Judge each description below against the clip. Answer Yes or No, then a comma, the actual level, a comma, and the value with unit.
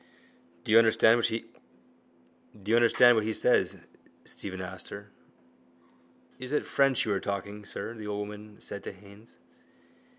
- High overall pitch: No, low, 105 Hz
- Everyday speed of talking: No, slow, 130 wpm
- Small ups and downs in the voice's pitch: Yes, narrow, 2.2 semitones